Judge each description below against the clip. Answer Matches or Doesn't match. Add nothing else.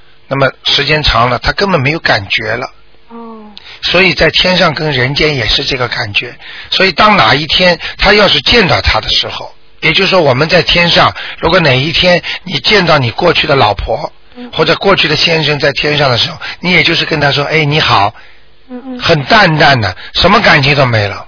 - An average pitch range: Matches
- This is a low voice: Doesn't match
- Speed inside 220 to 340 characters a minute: Matches